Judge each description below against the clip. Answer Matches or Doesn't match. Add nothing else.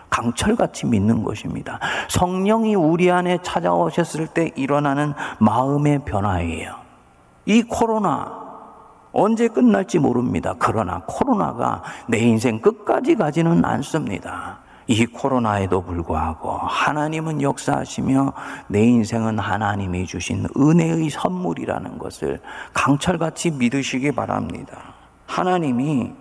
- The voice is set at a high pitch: Doesn't match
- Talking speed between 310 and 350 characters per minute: Doesn't match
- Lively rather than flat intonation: Matches